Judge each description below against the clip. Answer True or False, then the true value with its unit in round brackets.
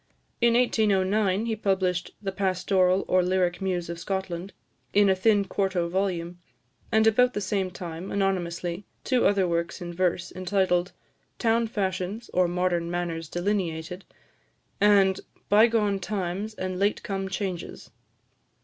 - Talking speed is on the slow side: True (130 wpm)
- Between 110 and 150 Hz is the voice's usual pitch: False (190 Hz)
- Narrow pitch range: True (2.3 semitones)